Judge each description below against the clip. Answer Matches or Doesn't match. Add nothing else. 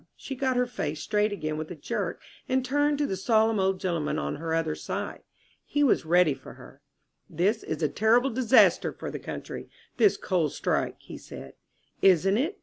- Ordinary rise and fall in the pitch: Doesn't match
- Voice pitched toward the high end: Matches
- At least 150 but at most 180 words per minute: Doesn't match